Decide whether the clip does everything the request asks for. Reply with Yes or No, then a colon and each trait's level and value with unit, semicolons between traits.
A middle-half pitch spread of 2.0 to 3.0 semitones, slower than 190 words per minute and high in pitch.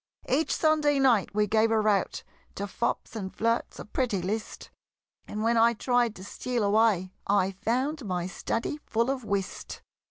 No: average, 3.4 semitones; average, 165 wpm; high, 225 Hz